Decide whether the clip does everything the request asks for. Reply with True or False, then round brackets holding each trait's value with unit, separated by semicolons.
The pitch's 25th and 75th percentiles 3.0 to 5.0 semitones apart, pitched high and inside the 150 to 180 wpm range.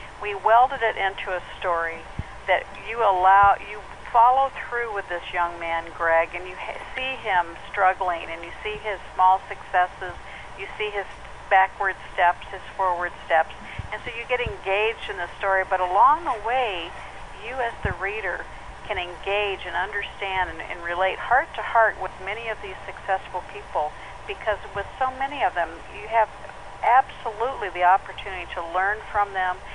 False (2.6 semitones; 195 Hz; 170 wpm)